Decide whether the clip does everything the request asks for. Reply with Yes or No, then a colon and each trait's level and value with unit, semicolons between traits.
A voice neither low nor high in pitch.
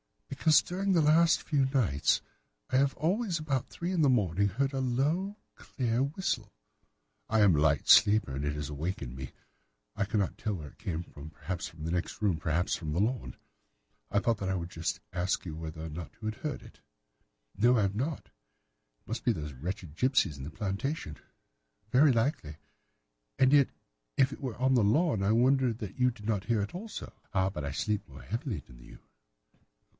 No: low, 105 Hz